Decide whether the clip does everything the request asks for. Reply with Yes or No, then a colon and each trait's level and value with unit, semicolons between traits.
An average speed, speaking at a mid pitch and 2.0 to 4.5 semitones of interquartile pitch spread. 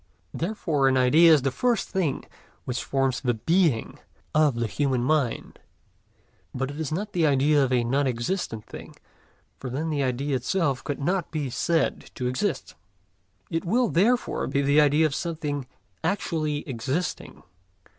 Yes: average, 155 wpm; medium, 145 Hz; average, 4.0 semitones